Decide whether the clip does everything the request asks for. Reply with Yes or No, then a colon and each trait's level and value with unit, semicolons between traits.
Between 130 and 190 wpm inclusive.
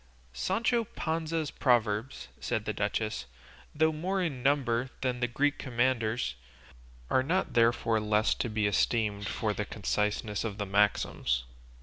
Yes: slow, 135 wpm